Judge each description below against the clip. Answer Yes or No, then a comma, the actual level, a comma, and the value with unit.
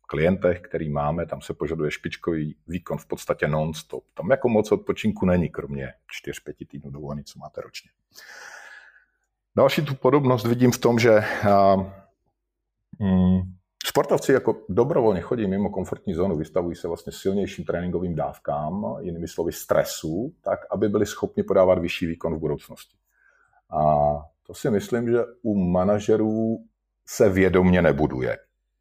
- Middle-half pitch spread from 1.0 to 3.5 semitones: No, wide, 5.4 semitones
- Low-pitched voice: Yes, very low, 90 Hz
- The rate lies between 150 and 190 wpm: No, average, 135 wpm